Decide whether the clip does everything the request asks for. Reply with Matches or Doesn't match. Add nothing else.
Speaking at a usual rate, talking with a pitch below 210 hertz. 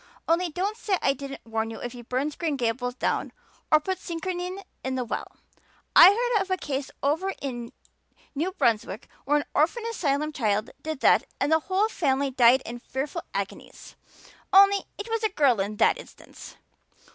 Doesn't match